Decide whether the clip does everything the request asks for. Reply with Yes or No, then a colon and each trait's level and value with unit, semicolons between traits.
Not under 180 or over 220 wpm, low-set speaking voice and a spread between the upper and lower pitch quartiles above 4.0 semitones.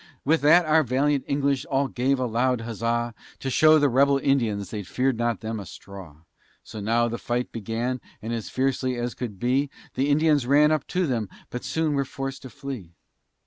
No: average, 195 wpm; low, 130 Hz; average, 3.2 semitones